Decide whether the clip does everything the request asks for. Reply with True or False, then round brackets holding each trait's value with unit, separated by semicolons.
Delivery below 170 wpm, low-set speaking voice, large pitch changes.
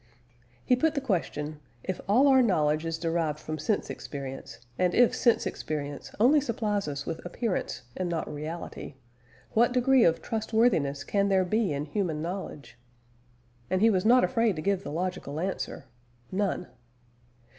False (155 wpm; 185 Hz; 6.4 semitones)